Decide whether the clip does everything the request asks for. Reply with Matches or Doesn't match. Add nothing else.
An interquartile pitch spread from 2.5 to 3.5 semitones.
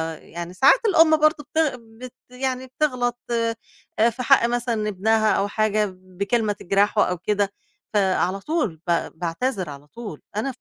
Doesn't match